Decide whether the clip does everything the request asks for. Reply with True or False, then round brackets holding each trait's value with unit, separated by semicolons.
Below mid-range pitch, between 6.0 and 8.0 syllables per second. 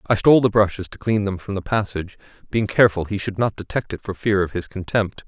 True (100 Hz; 6.2 syllables/s)